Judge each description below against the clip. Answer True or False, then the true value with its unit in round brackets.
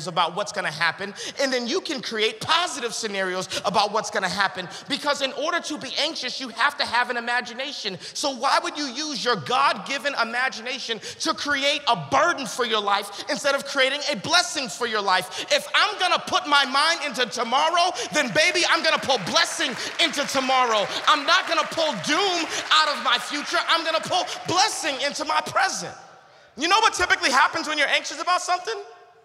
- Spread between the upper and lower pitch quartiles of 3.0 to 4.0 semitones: False (5.1 semitones)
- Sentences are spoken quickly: False (190 wpm)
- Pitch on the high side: True (280 Hz)